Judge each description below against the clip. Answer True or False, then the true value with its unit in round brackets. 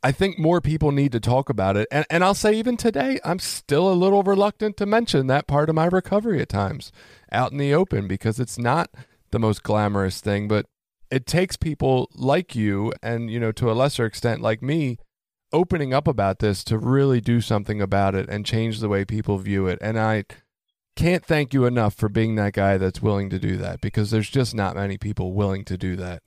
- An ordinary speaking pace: False (220 wpm)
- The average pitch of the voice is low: True (115 Hz)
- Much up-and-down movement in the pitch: True (6.4 semitones)